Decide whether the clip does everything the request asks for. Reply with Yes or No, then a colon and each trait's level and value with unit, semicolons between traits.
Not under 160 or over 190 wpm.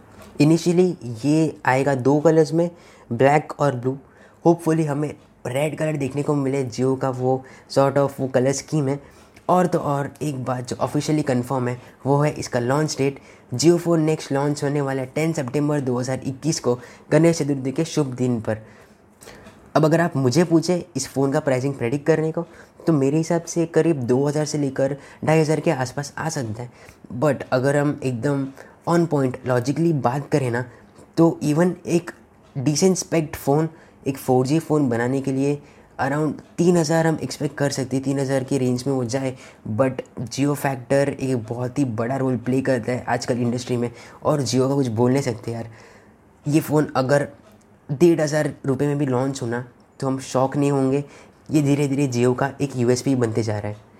Yes: average, 185 wpm